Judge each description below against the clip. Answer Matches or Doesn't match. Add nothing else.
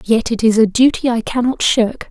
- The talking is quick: Matches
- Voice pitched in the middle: Doesn't match